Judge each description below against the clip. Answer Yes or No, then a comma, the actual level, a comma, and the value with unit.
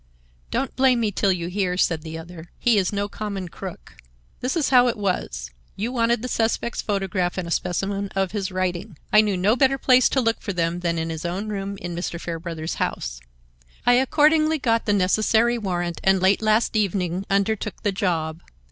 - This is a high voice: Yes, high, 195 Hz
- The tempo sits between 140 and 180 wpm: No, average, 195 wpm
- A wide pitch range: No, average, 4.3 semitones